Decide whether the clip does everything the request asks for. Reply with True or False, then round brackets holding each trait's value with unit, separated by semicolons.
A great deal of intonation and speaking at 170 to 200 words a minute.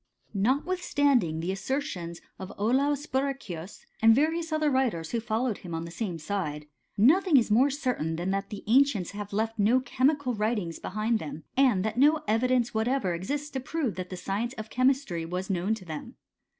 True (6.2 semitones; 180 wpm)